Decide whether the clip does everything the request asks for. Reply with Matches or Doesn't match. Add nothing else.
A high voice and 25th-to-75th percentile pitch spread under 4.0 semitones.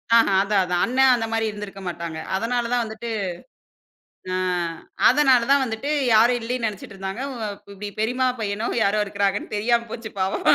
Matches